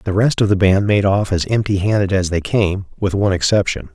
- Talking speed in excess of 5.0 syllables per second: Yes, 5.6 syllables/s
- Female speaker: No, male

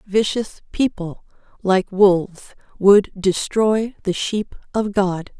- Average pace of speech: No, slow, 110 wpm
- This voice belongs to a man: No, female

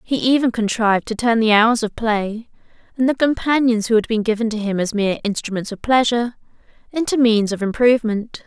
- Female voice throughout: Yes, female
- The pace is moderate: Yes, average, 190 wpm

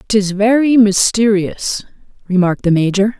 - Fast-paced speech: No, slow, 115 wpm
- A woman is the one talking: Yes, female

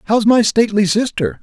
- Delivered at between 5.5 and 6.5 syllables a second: Yes, 5.7 syllables/s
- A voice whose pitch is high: Yes, high, 205 Hz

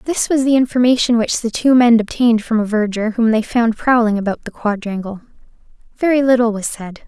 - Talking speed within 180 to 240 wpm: Yes, average, 195 wpm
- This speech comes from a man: No, female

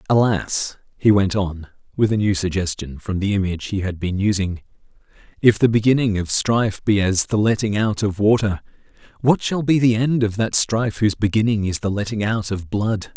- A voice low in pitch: Yes, low, 105 Hz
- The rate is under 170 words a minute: No, average, 195 wpm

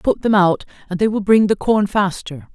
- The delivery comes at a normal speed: No, fast, 235 wpm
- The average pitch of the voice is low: No, high, 200 Hz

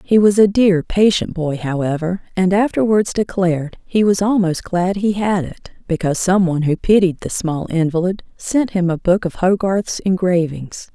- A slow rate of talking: No, average, 175 wpm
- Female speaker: Yes, female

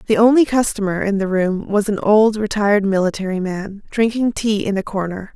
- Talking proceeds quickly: No, average, 190 wpm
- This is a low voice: No, high, 205 Hz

